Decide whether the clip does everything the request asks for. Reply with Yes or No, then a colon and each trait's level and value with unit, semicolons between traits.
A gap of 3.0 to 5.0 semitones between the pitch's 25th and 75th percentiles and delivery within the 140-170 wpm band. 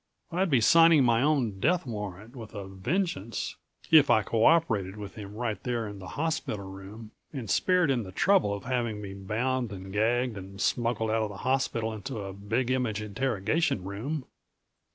No: average, 4.5 semitones; average, 180 wpm